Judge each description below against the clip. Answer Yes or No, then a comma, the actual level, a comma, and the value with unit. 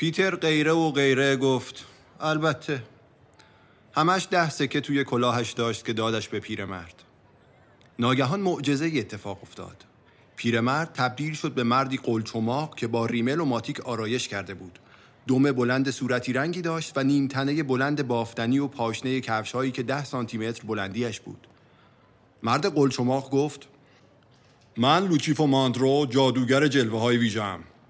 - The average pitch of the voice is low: Yes, low, 130 Hz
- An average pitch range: Yes, average, 3.5 semitones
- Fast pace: No, average, 135 wpm